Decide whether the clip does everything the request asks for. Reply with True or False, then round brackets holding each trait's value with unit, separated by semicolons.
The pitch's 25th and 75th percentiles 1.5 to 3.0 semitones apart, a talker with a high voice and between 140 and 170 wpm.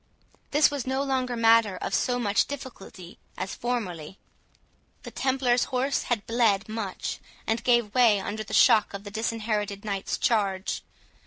False (3.6 semitones; 225 Hz; 150 wpm)